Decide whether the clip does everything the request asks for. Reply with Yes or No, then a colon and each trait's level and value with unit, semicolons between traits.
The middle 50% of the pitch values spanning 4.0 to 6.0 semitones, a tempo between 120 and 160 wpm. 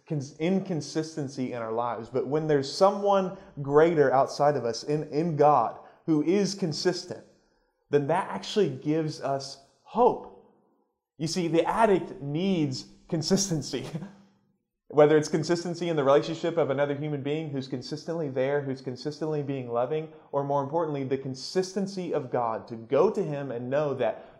No: average, 3.6 semitones; average, 150 wpm